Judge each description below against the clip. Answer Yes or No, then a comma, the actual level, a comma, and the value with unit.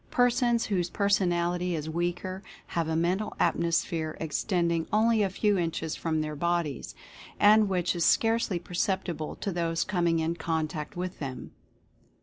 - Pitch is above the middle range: No, medium, 175 Hz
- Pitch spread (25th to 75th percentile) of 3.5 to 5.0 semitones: No, average, 3.0 semitones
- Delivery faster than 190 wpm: No, average, 140 wpm